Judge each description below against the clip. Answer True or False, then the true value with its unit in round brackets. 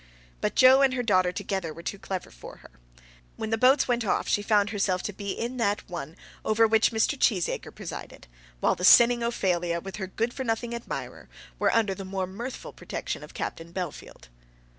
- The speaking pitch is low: False (205 Hz)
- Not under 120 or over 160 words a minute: False (195 wpm)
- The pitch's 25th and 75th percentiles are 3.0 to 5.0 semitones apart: True (4.1 semitones)